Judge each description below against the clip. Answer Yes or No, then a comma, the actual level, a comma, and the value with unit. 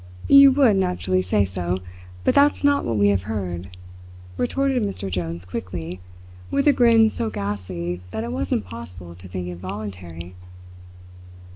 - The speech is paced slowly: No, average, 150 wpm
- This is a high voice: No, very low, 95 Hz